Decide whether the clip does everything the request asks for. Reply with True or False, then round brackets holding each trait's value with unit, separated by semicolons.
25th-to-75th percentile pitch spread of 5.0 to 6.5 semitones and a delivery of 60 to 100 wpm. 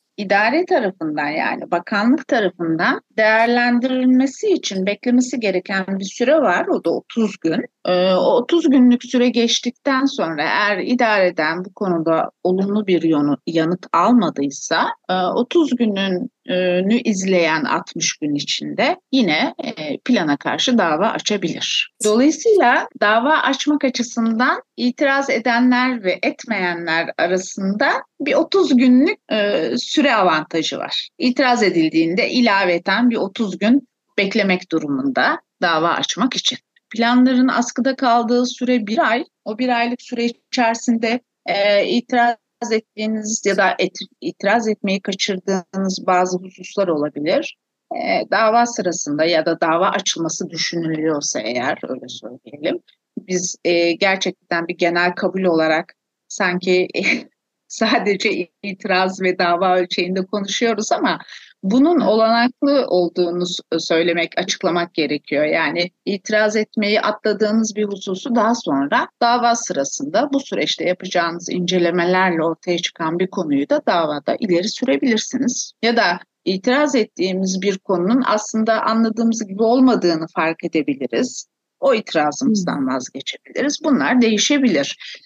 False (5.5 semitones; 115 wpm)